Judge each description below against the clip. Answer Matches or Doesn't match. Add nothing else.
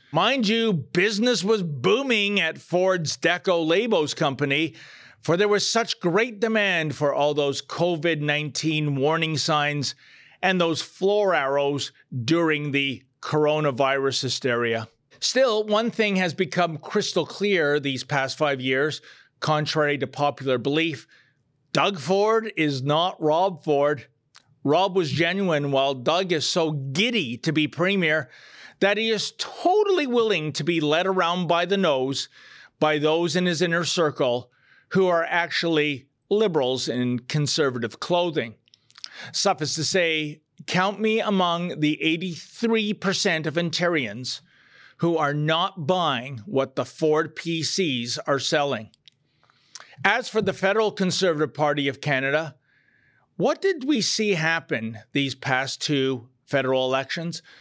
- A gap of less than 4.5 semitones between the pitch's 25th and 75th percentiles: Doesn't match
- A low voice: Doesn't match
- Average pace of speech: Doesn't match